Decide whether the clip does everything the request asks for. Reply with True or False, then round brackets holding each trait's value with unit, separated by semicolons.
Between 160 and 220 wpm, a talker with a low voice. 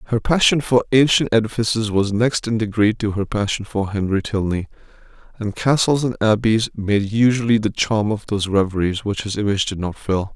True (180 wpm; 110 Hz)